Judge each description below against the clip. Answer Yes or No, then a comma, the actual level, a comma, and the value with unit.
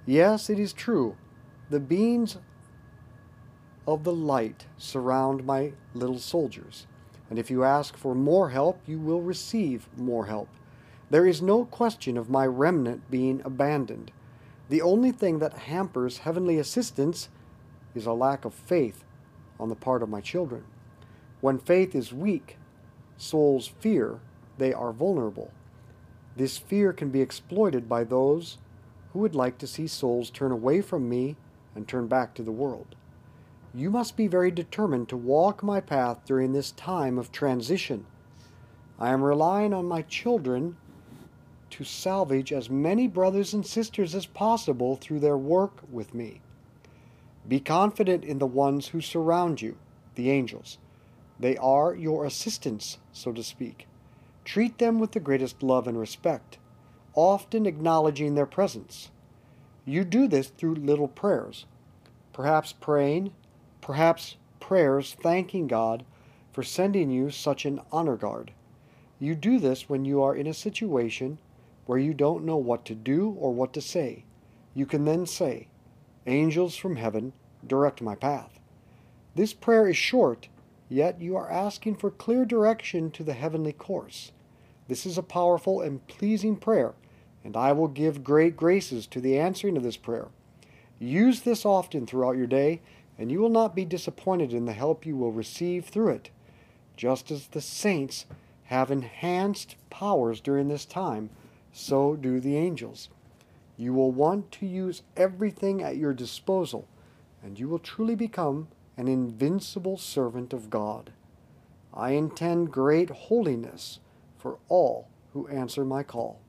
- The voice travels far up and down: Yes, wide, 5.9 semitones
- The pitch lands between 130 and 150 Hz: Yes, medium, 140 Hz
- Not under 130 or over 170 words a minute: Yes, average, 150 wpm